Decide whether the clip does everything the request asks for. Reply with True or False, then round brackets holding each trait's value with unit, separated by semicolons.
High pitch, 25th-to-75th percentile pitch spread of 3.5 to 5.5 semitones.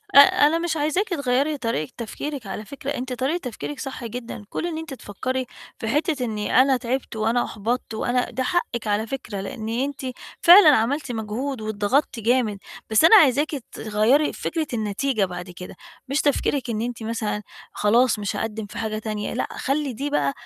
True (245 Hz; 4.6 semitones)